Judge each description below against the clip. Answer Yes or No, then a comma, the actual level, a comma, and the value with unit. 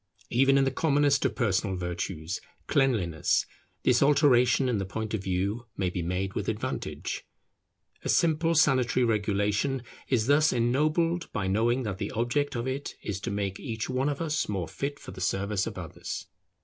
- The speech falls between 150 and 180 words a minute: Yes, average, 175 wpm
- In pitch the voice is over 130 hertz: No, low, 120 Hz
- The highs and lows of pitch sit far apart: Yes, wide, 6.0 semitones